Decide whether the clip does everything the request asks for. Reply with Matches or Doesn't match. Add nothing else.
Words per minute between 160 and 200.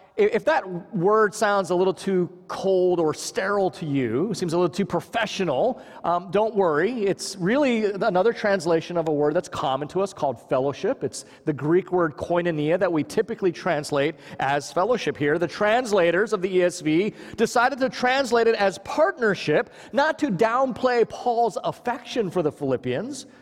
Matches